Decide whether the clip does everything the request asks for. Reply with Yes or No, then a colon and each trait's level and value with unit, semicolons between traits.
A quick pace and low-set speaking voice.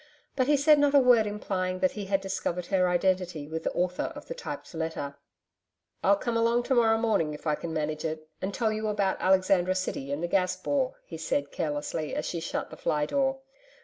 No: fast, 215 wpm; medium, 185 Hz